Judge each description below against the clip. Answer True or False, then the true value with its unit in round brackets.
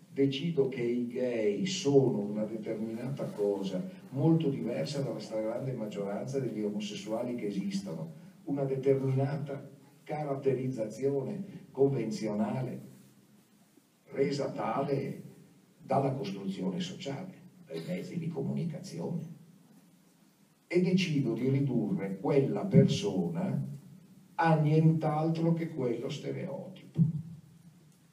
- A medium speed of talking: False (85 wpm)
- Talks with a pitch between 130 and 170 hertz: True (140 Hz)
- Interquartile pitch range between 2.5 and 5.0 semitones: False (5.5 semitones)